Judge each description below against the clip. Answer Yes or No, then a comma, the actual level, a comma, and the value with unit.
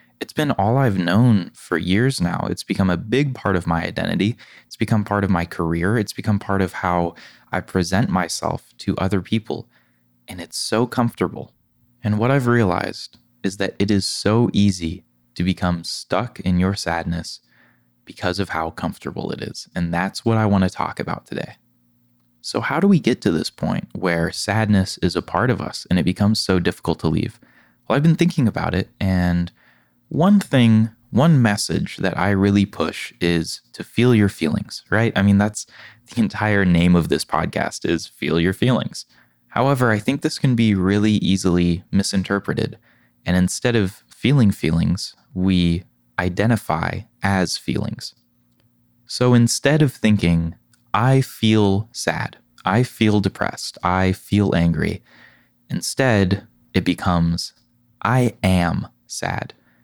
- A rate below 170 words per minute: Yes, average, 160 wpm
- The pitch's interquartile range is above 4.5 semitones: Yes, average, 4.9 semitones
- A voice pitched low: Yes, low, 100 Hz